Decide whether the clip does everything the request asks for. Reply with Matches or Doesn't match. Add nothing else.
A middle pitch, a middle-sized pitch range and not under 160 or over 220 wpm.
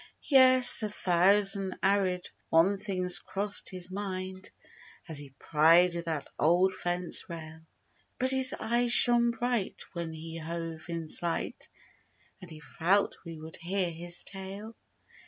Doesn't match